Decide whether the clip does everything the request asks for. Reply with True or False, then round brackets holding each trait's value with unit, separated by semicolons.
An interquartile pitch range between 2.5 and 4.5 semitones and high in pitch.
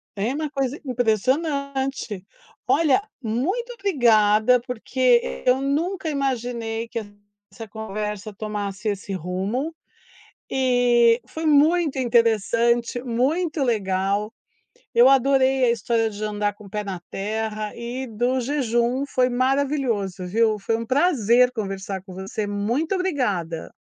True (4.2 semitones; 235 Hz)